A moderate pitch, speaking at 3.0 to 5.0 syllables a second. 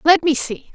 No: very high, 305 Hz; 4.7 syllables/s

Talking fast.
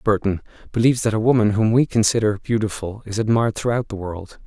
No: average, 190 wpm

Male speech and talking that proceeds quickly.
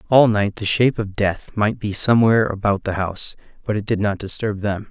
Yes: male; fast, 220 wpm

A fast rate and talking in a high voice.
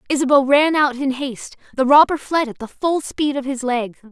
Yes: fast, 220 wpm; very high, 270 Hz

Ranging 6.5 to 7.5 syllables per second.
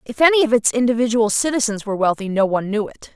Yes: 7.0 syllables/s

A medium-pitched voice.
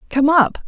No: very high, 285 Hz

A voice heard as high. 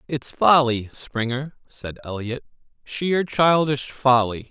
No: low, 130 Hz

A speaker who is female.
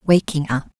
Yes: female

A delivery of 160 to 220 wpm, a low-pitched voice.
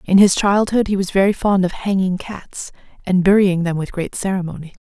No: average, 200 wpm; high, 190 Hz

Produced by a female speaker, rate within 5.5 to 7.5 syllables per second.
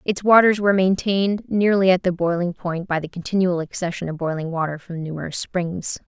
Yes: female; 5.6 syllables/s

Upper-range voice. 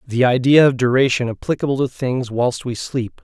No: low, 125 Hz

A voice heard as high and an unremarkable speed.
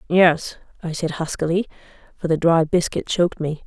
No: medium, 165 Hz; average, 165 wpm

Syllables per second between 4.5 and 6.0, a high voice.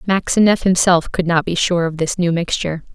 No: 5.5 syllables/s; medium, 175 Hz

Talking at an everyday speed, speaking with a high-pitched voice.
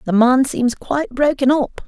Yes: average, 190 wpm; very high, 260 Hz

